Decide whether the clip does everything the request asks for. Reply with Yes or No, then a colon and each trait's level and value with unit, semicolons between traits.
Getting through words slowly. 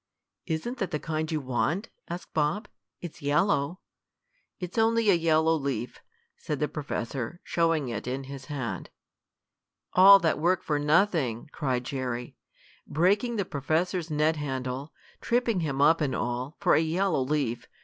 No: average, 150 wpm